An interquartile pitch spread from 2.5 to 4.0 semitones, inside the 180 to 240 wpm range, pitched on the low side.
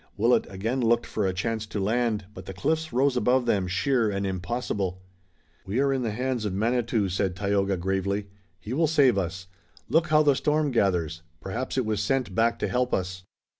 No: average, 4.7 semitones; average, 195 wpm; low, 110 Hz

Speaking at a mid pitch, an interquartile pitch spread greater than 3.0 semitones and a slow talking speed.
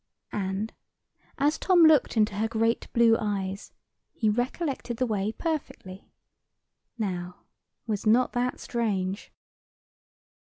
No: high, 225 Hz; average, 3.8 semitones; slow, 110 wpm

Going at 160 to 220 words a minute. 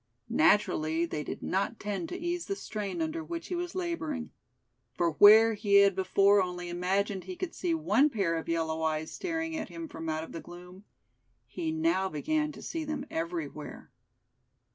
Yes: average, 175 wpm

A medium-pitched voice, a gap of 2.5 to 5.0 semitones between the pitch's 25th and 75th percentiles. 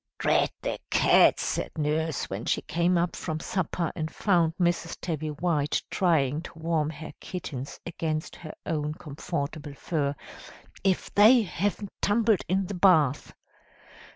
Yes: medium, 165 Hz; average, 3.1 semitones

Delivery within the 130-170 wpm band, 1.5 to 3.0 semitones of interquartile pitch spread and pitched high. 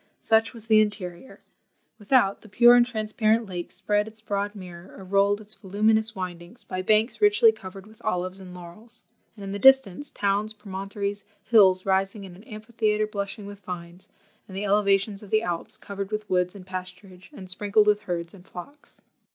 No: average, 180 wpm; narrow, 2.5 semitones; high, 200 Hz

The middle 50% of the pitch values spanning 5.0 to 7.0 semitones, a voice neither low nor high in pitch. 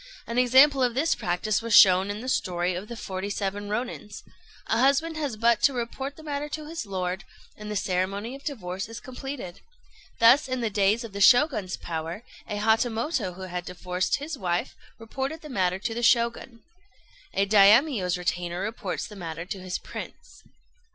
No: wide, 5.4 semitones; high, 215 Hz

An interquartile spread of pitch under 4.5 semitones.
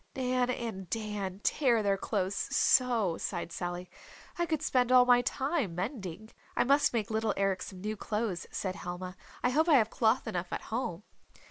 No: average, 4.9 semitones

